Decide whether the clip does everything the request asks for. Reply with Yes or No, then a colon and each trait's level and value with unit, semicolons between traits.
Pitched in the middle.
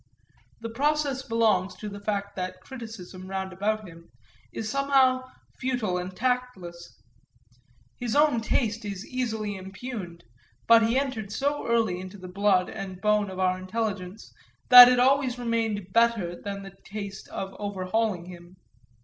No: high, 210 Hz